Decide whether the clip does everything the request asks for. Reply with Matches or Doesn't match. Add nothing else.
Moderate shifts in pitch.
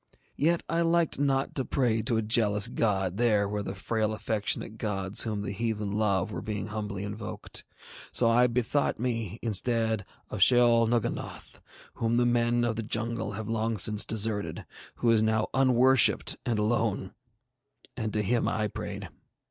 Doesn't match